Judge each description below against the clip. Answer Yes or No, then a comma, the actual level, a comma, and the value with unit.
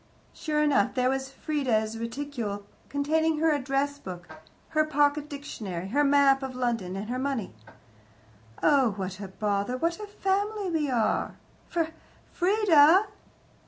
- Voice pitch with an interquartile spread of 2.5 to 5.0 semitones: No, wide, 5.5 semitones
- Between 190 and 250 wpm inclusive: No, slow, 135 wpm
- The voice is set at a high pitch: Yes, very high, 275 Hz